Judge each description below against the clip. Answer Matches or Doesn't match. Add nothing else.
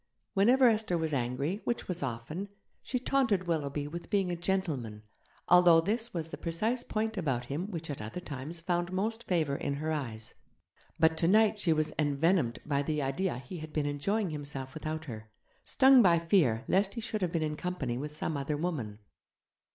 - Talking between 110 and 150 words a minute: Doesn't match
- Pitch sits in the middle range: Matches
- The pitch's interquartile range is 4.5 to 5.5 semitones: Matches